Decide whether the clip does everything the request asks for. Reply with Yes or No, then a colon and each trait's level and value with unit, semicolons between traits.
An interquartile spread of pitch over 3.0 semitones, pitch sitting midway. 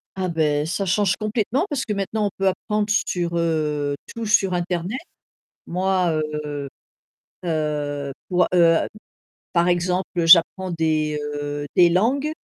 Yes: average, 3.8 semitones; medium, 175 Hz